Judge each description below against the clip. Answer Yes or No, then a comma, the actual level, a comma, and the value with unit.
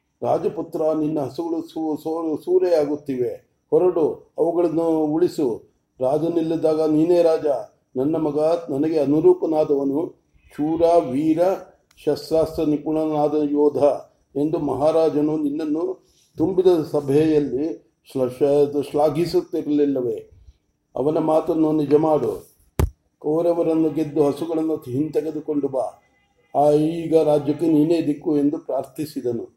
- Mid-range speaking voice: Yes, medium, 155 Hz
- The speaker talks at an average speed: No, slow, 90 wpm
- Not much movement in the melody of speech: Yes, narrow, 2.0 semitones